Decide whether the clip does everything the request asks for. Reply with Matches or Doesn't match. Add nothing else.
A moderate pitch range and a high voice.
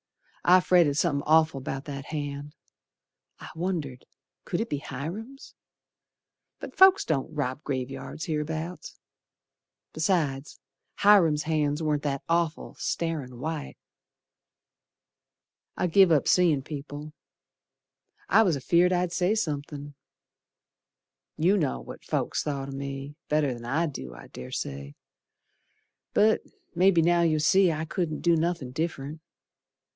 Doesn't match